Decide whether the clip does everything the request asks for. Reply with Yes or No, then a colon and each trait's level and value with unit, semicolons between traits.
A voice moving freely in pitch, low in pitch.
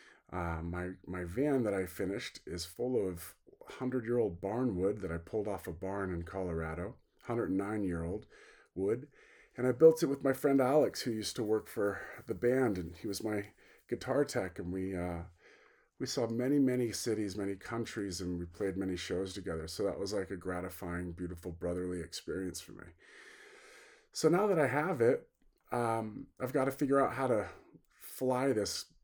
Yes: wide, 6.1 semitones; low, 100 Hz